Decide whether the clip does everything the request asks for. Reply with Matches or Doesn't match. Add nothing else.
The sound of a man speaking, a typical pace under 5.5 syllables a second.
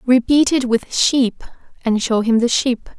Doesn't match